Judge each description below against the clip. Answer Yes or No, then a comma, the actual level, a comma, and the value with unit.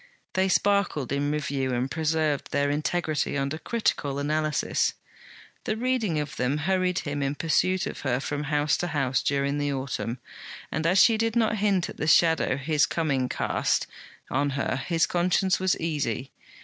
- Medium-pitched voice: Yes, medium, 150 Hz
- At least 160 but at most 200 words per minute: Yes, average, 165 wpm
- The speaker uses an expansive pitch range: No, average, 4.3 semitones